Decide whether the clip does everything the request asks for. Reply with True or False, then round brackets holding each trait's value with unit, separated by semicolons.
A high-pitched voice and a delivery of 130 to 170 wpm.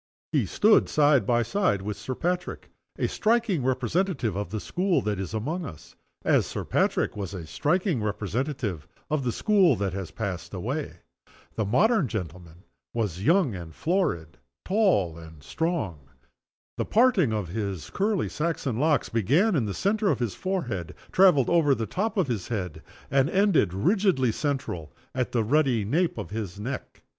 False (125 Hz; 165 wpm)